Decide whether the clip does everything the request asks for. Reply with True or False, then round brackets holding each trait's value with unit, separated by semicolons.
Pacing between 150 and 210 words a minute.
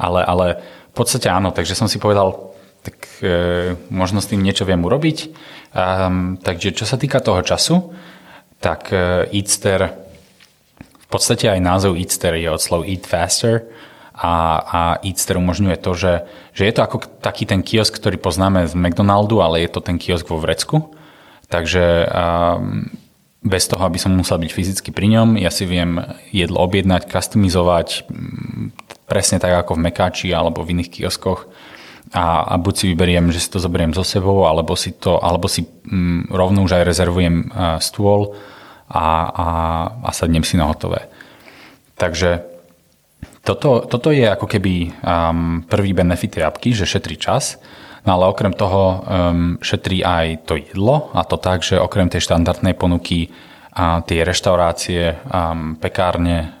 True (160 wpm)